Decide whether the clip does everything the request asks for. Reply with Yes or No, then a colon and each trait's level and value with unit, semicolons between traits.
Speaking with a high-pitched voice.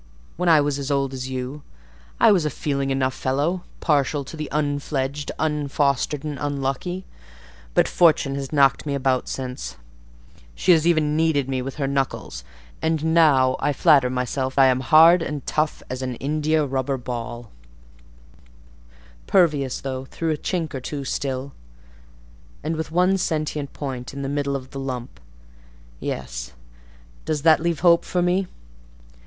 No: medium, 140 Hz